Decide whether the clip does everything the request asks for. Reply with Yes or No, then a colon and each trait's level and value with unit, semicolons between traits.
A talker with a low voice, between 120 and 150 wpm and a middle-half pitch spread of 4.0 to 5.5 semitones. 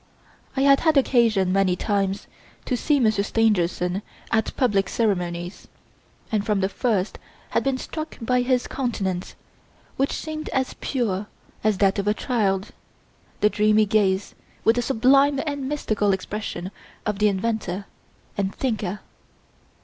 No: high, 215 Hz; average, 140 wpm; average, 4.5 semitones